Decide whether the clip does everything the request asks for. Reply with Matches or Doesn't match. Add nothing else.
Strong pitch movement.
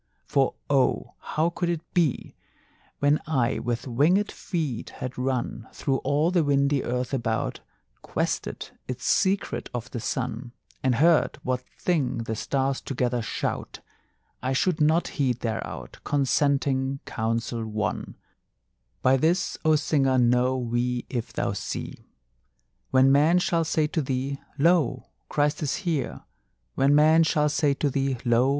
Doesn't match